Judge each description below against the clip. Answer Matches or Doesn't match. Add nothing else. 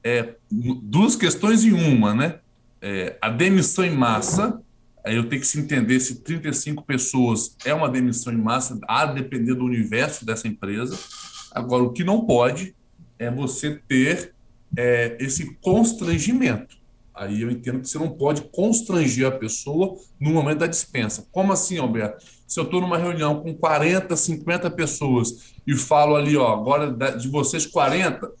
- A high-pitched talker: Doesn't match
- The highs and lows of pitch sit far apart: Matches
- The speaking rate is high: Doesn't match